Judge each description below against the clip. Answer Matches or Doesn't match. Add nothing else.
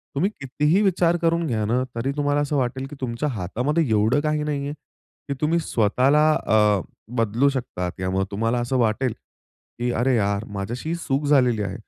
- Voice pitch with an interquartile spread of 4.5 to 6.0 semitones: Matches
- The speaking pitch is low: Matches